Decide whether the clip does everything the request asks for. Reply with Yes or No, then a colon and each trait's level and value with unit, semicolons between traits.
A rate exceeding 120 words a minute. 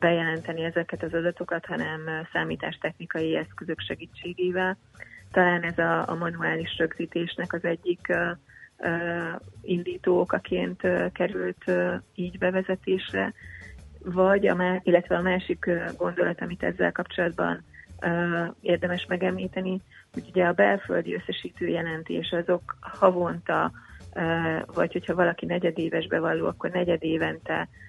No: average, 115 wpm